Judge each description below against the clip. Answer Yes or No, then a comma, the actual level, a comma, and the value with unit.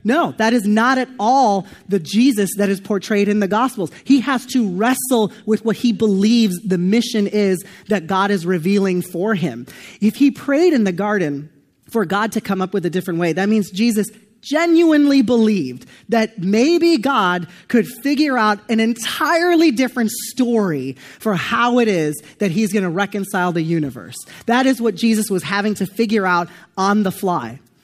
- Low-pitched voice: No, high, 210 Hz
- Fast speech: No, average, 180 wpm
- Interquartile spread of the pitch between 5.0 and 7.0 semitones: No, average, 4.1 semitones